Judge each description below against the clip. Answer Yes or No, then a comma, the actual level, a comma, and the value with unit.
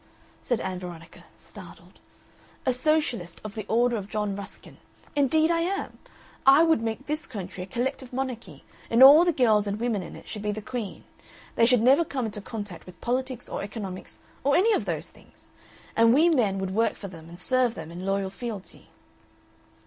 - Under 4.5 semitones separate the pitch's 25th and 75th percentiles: No, average, 5.0 semitones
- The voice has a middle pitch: No, high, 230 Hz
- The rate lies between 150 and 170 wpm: No, average, 190 wpm